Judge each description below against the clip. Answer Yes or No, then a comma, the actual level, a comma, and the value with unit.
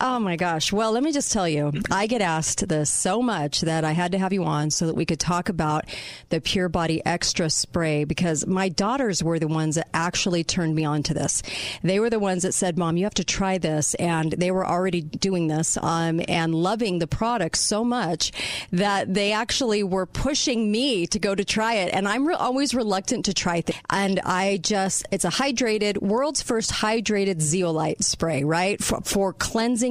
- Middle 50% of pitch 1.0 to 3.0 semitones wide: No, average, 4.5 semitones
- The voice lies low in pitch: No, medium, 185 Hz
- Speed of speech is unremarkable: No, fast, 215 wpm